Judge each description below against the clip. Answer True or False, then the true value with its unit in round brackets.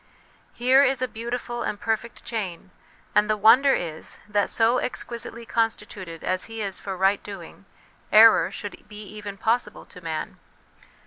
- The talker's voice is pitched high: True (215 Hz)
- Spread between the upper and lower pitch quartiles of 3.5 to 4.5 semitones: False (3.0 semitones)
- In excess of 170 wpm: False (155 wpm)